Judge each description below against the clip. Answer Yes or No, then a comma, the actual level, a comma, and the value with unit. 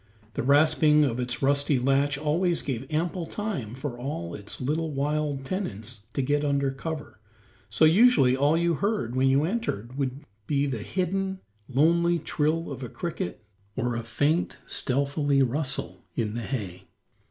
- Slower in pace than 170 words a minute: Yes, average, 155 wpm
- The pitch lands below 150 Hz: Yes, medium, 140 Hz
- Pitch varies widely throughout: No, average, 3.8 semitones